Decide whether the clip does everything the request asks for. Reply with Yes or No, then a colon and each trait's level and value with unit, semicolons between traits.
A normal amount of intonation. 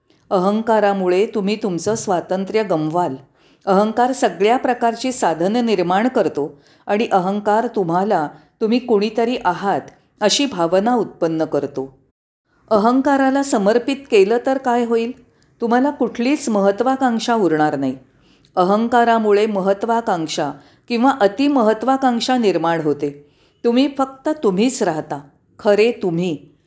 No: wide, 6.2 semitones